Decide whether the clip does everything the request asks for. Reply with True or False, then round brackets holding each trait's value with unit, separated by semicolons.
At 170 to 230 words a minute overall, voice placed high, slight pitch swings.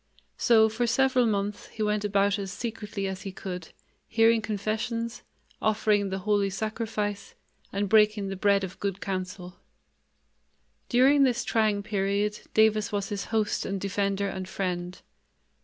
False (140 wpm; 205 Hz; 1.9 semitones)